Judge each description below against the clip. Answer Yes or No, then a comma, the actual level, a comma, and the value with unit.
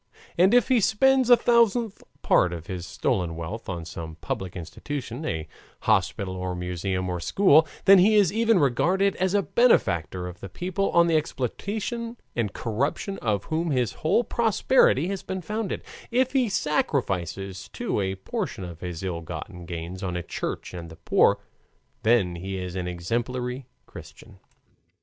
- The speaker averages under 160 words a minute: No, average, 165 wpm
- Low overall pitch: Yes, low, 120 Hz